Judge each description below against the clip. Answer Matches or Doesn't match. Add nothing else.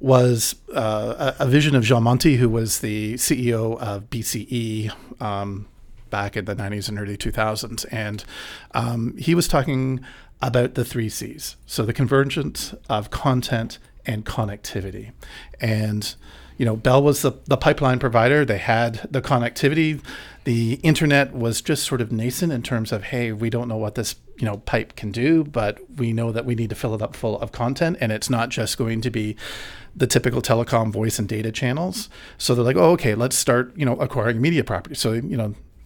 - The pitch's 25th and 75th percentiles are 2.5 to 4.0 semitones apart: Matches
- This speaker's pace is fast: Doesn't match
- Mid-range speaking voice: Doesn't match